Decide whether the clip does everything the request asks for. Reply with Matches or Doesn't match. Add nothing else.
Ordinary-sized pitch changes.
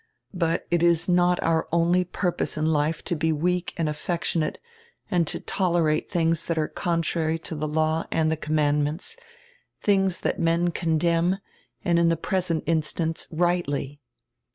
Doesn't match